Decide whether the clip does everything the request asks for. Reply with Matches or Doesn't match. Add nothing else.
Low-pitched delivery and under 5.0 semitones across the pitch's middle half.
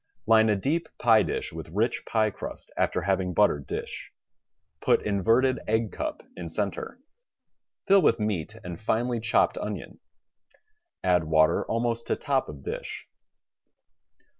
Matches